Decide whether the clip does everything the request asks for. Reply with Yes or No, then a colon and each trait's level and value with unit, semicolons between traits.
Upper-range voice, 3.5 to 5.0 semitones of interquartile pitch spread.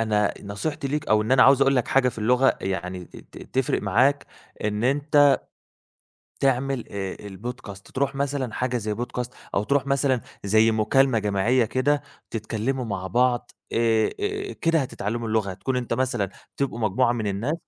No: low, 120 Hz; average, 4.2 semitones